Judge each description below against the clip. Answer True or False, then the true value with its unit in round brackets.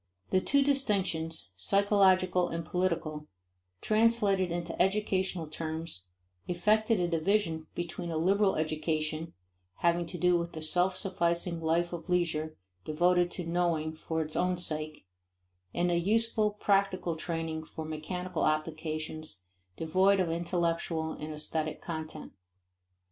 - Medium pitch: True (170 Hz)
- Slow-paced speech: True (125 wpm)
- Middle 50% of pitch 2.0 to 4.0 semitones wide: True (2.8 semitones)